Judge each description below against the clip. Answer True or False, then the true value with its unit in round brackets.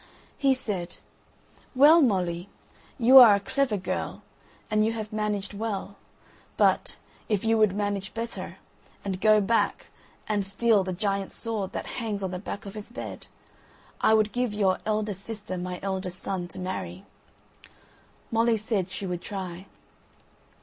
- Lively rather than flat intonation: False (2.8 semitones)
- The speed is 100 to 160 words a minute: True (150 wpm)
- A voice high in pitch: True (205 Hz)